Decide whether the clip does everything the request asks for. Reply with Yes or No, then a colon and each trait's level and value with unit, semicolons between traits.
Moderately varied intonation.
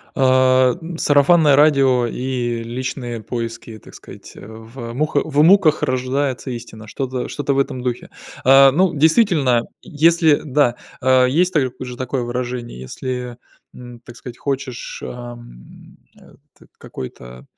Yes: average, 3.0 semitones